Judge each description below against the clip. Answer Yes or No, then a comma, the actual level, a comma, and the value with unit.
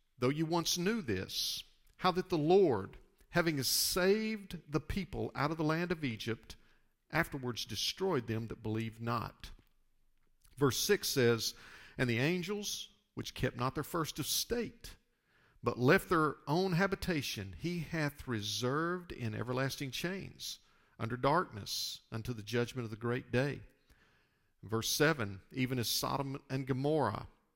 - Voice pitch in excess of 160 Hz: No, medium, 140 Hz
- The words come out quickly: No, average, 140 wpm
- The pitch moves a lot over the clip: Yes, wide, 6.6 semitones